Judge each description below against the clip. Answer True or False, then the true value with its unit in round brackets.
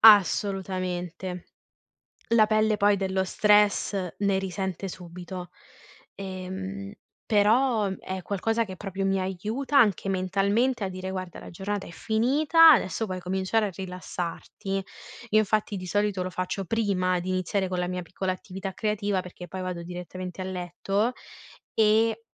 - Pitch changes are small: True (2.3 semitones)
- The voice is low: False (195 Hz)